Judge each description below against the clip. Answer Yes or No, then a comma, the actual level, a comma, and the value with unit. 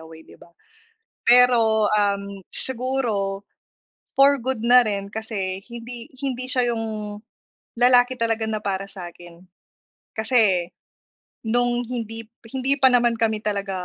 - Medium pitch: No, high, 225 Hz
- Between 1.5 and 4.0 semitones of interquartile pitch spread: Yes, average, 3.6 semitones